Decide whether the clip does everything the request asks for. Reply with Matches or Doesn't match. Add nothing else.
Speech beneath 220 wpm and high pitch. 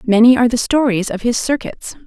Matches